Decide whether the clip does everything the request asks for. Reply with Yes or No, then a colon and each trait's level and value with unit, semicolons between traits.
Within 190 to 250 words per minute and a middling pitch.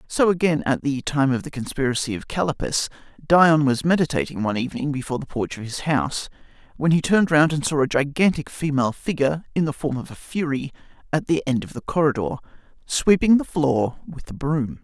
Yes: average, 200 wpm; medium, 145 Hz